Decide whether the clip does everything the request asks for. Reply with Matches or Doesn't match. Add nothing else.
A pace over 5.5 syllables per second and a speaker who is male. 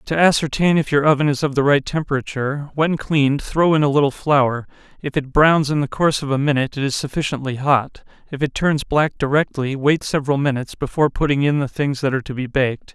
Matches